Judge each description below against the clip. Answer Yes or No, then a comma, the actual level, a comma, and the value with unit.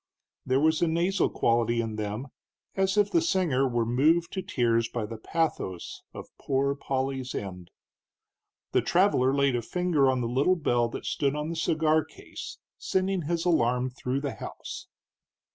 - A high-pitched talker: No, low, 135 Hz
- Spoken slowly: No, average, 165 wpm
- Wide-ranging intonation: Yes, wide, 5.8 semitones